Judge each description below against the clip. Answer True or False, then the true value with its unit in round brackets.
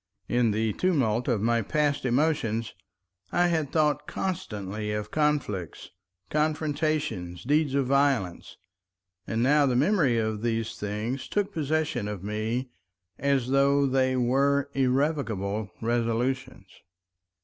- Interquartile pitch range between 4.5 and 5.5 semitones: True (4.9 semitones)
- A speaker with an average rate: False (115 wpm)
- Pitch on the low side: True (130 Hz)